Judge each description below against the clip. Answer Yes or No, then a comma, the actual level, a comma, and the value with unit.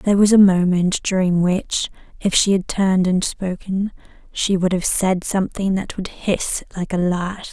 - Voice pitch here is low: No, medium, 185 Hz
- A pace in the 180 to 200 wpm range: Yes, average, 185 wpm